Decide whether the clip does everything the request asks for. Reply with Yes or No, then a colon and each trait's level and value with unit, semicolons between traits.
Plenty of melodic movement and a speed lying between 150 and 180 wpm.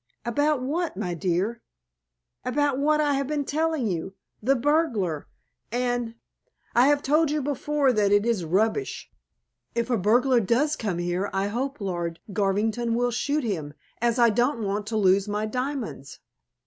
Yes: wide, 5.8 semitones; average, 160 wpm